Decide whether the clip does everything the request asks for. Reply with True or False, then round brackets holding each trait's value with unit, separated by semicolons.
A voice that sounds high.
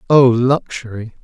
False (125 Hz)